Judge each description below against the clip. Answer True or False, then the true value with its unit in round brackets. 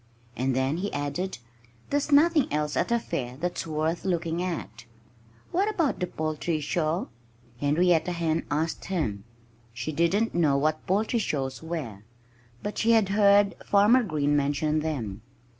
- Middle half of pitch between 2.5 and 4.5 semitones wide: False (5.5 semitones)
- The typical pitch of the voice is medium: True (160 Hz)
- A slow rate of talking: False (145 wpm)